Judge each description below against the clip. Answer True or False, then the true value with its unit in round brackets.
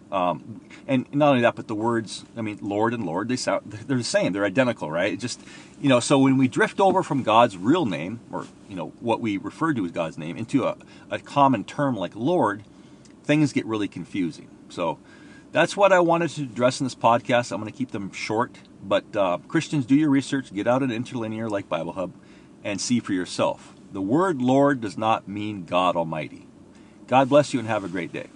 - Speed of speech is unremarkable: False (220 wpm)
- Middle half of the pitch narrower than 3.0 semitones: False (4.0 semitones)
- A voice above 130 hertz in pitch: False (125 Hz)